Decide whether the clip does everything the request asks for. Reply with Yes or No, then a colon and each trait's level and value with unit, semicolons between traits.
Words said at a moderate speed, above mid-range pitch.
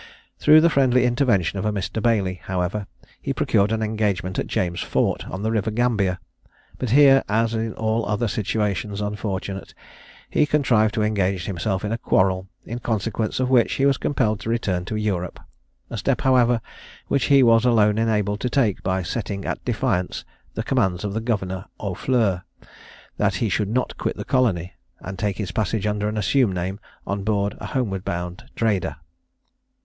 No: average, 175 wpm; low, 105 Hz